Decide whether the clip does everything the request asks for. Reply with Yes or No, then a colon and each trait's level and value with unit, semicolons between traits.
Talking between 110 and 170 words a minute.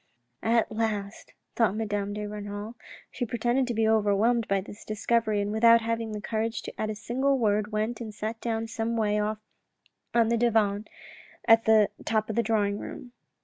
No: average, 190 wpm